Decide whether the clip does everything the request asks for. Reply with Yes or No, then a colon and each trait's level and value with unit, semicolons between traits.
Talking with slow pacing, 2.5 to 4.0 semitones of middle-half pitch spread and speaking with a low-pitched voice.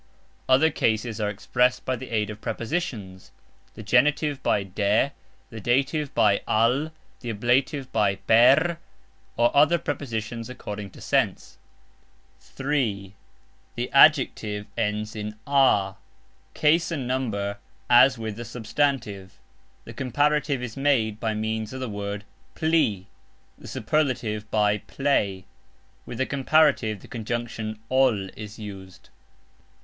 No: slow, 125 wpm; average, 4.4 semitones; low, 115 Hz